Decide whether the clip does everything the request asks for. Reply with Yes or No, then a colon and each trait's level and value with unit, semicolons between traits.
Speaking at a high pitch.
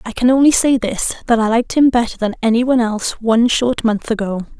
Yes: high, 235 Hz